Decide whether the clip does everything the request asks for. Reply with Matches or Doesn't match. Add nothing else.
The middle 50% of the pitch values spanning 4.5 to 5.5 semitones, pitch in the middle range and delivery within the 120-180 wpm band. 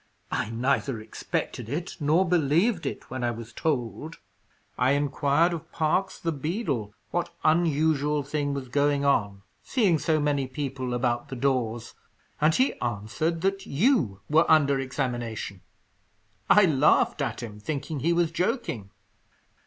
Matches